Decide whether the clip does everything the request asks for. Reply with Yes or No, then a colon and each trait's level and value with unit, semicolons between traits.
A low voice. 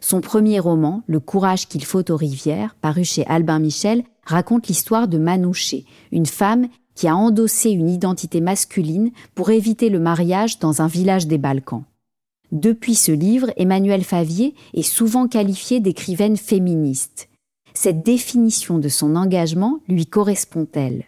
No: medium, 185 Hz